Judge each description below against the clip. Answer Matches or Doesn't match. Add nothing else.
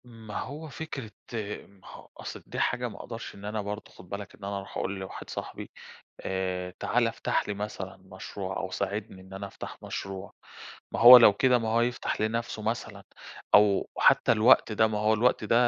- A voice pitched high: Doesn't match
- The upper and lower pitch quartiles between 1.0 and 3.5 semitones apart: Matches